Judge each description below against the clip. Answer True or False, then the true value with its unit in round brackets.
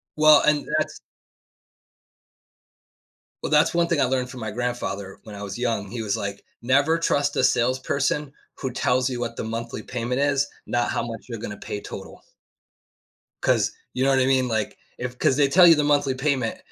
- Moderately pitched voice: False (125 Hz)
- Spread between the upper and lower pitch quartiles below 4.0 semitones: True (3.6 semitones)